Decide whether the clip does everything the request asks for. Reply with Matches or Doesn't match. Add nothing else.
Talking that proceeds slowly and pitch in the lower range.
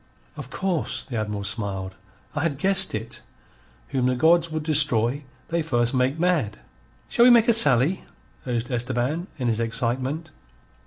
Doesn't match